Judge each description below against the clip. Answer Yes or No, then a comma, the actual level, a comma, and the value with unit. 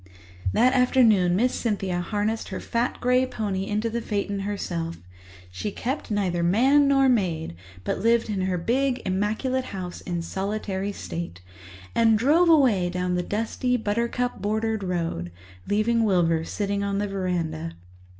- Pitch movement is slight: No, average, 4.7 semitones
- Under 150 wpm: Yes, average, 140 wpm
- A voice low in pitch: No, high, 205 Hz